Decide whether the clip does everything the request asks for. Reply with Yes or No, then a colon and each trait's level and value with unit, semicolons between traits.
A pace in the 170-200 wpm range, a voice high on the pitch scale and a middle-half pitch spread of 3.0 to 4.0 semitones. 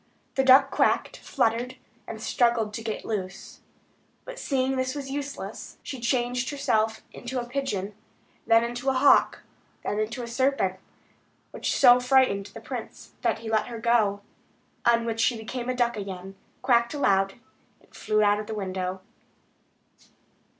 No: average, 155 wpm; high, 235 Hz; average, 3.4 semitones